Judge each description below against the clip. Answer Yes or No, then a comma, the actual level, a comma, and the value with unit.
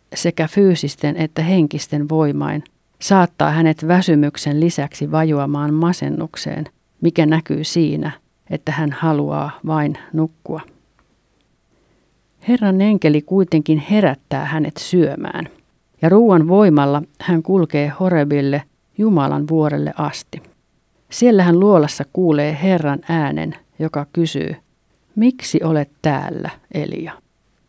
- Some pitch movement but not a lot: Yes, average, 3.1 semitones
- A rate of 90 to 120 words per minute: Yes, average, 100 wpm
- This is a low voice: No, medium, 160 Hz